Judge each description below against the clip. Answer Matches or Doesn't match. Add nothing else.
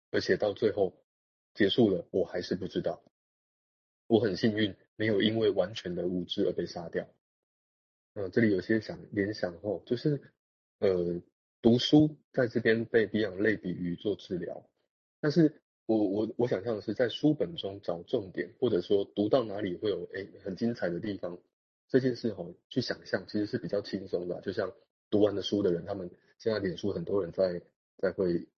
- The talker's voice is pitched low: Matches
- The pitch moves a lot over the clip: Doesn't match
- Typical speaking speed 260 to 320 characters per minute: Matches